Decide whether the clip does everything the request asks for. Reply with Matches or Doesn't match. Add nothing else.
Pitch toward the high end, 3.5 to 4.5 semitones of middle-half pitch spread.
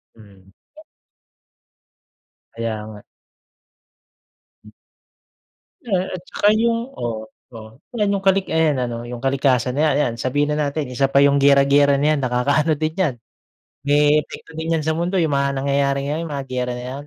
Doesn't match